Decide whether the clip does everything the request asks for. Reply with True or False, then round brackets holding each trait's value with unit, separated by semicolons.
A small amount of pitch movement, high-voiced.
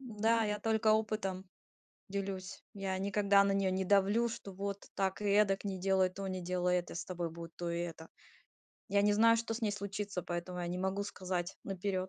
True (1.9 semitones; 195 Hz)